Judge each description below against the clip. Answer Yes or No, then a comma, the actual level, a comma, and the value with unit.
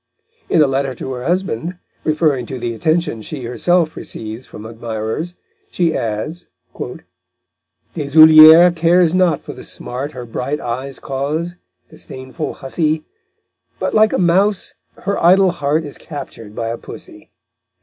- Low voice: No, medium, 150 Hz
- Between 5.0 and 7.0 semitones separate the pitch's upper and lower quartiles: Yes, wide, 5.4 semitones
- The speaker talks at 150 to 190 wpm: No, average, 140 wpm